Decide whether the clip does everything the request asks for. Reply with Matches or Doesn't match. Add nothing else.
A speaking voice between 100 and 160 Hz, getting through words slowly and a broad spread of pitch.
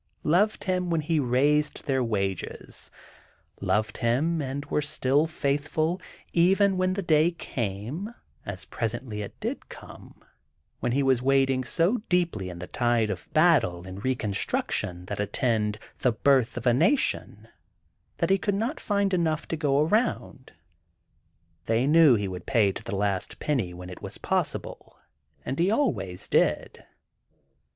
Doesn't match